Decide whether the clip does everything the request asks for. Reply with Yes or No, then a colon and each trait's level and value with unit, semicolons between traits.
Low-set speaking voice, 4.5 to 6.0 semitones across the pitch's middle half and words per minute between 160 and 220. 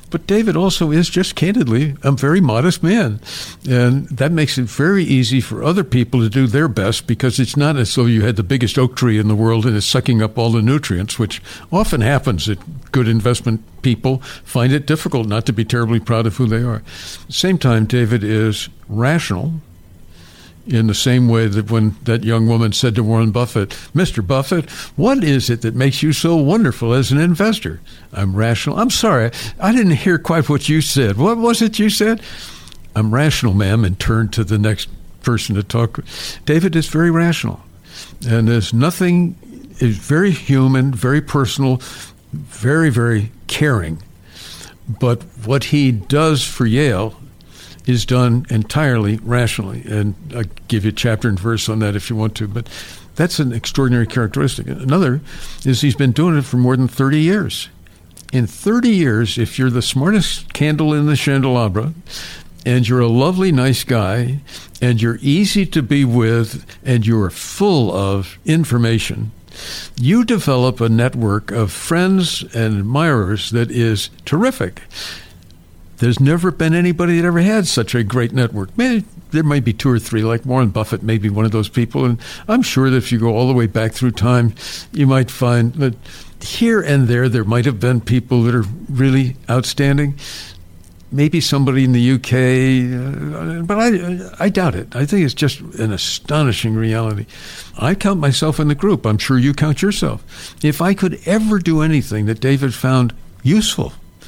Yes: low, 125 Hz; average, 4.9 semitones; average, 180 wpm